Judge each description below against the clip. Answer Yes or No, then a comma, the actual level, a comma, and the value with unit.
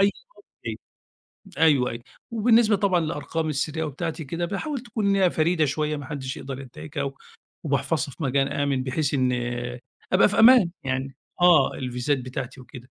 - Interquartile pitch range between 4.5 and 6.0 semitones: Yes, average, 5.0 semitones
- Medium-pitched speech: Yes, medium, 150 Hz